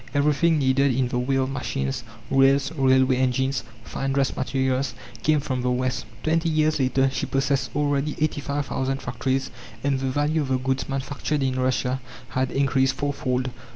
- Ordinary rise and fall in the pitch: No, narrow, 1.5 semitones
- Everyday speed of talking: Yes, average, 160 wpm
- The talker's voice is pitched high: No, low, 135 Hz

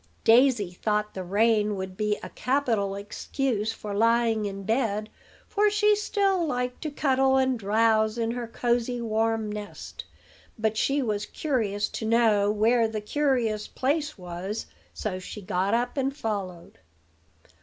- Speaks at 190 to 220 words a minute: No, average, 145 wpm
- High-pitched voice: Yes, high, 225 Hz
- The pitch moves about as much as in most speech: Yes, average, 3.5 semitones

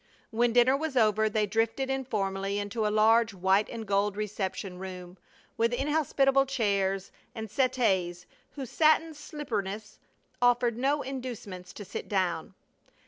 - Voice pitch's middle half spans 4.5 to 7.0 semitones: Yes, average, 4.8 semitones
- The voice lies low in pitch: No, high, 220 Hz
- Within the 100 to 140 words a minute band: Yes, slow, 135 wpm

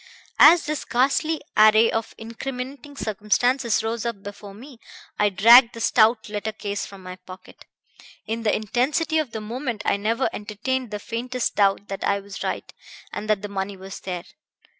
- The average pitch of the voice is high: Yes, high, 220 Hz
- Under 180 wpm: Yes, average, 170 wpm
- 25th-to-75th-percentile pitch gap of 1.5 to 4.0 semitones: Yes, average, 3.5 semitones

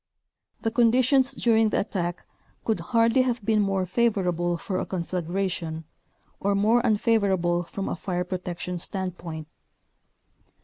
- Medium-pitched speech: No, high, 195 Hz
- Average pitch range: Yes, average, 4.4 semitones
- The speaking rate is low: Yes, slow, 125 wpm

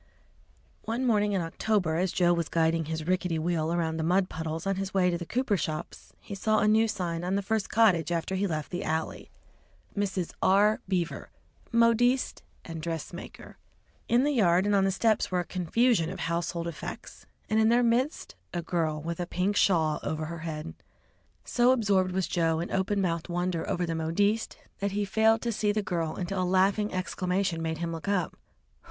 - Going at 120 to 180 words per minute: No, average, 195 wpm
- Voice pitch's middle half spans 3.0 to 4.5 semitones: Yes, average, 3.8 semitones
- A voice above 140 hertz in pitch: Yes, medium, 185 Hz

